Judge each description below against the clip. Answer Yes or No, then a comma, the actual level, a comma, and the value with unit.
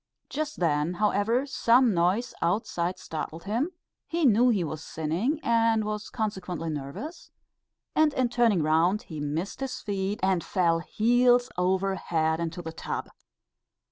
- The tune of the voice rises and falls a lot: Yes, wide, 6.0 semitones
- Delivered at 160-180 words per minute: No, average, 140 wpm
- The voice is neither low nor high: No, high, 195 Hz